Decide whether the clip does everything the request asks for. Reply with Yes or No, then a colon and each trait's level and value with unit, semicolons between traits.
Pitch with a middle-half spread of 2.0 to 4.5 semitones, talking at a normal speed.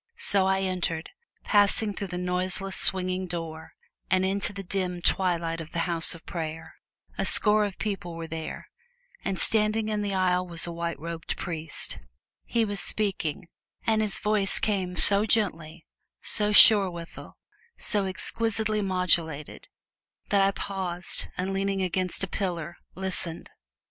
Yes: average, 2.9 semitones; average, 150 wpm